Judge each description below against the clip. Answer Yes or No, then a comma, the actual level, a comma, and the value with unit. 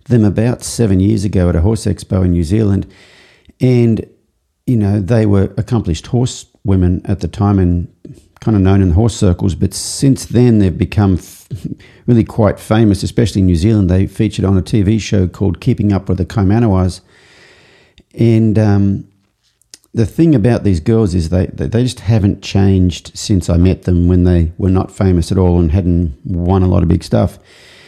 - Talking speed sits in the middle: Yes, average, 185 wpm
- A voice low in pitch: Yes, low, 100 Hz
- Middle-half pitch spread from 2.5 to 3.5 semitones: Yes, average, 3.2 semitones